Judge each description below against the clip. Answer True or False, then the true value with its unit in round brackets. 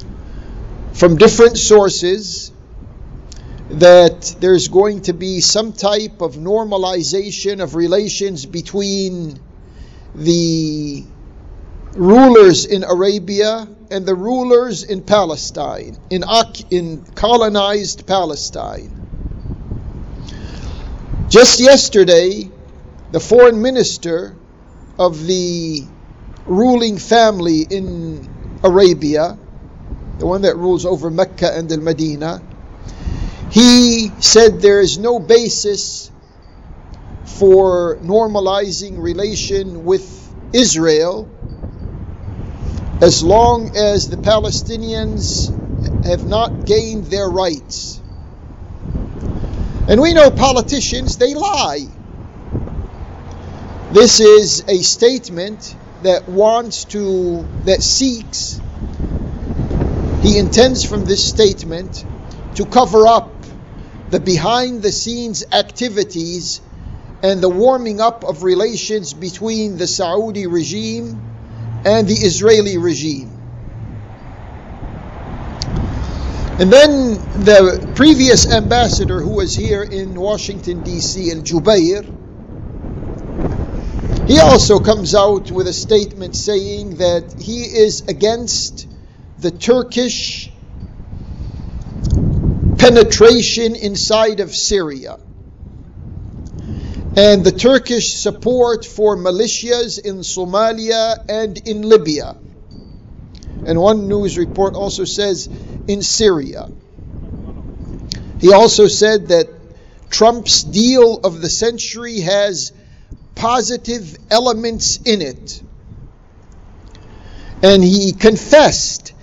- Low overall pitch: False (190 Hz)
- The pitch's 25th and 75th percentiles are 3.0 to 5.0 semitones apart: False (5.6 semitones)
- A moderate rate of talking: False (90 wpm)